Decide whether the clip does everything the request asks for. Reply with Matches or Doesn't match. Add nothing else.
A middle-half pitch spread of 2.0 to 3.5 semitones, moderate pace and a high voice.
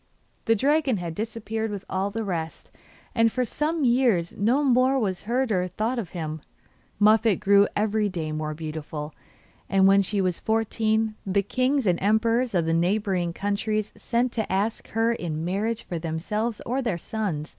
Doesn't match